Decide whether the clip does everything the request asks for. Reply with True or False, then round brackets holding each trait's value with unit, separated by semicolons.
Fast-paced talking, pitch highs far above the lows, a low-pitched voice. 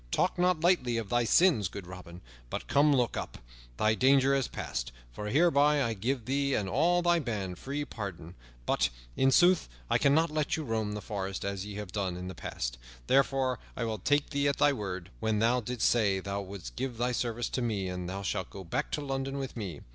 True (215 wpm; 5.9 semitones; 115 Hz)